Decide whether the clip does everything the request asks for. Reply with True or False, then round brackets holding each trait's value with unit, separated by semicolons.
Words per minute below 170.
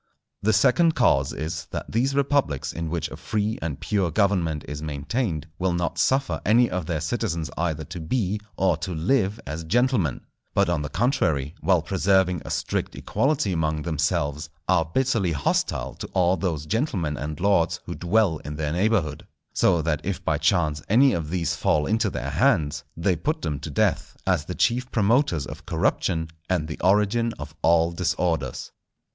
False (175 wpm)